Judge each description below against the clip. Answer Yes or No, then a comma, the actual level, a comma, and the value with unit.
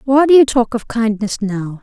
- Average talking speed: No, fast, 230 wpm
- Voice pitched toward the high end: Yes, high, 230 Hz